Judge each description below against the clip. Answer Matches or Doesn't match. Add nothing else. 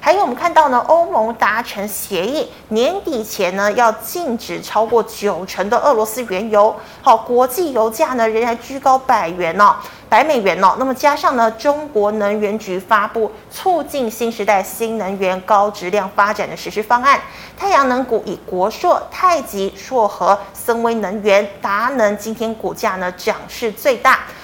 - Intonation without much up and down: Doesn't match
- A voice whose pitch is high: Matches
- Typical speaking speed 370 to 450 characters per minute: Doesn't match